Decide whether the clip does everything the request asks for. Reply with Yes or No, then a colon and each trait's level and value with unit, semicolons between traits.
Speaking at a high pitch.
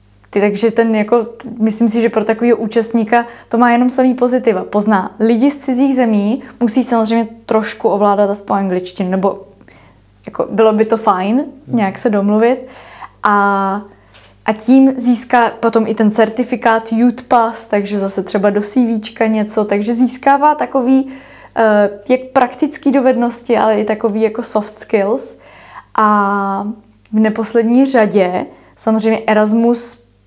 Yes: high, 225 Hz